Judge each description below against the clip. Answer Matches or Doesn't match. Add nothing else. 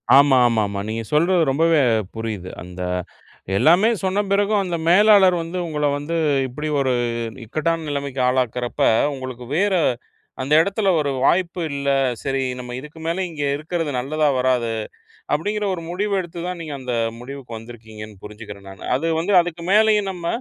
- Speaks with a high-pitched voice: Doesn't match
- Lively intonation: Matches